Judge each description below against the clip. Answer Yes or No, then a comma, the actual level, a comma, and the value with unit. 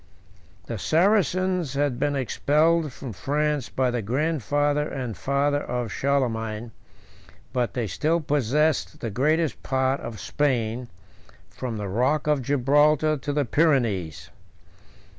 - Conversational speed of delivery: No, slow, 125 wpm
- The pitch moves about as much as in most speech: Yes, average, 3.9 semitones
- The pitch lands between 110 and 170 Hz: Yes, medium, 140 Hz